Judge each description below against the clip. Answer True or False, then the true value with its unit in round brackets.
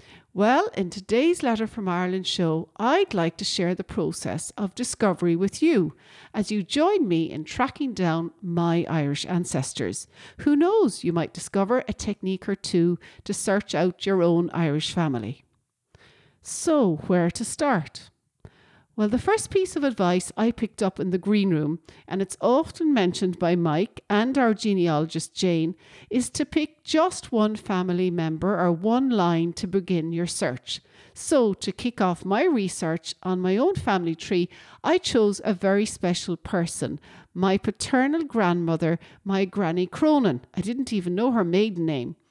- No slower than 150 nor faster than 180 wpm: True (160 wpm)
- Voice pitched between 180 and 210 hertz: True (190 Hz)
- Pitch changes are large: False (4.7 semitones)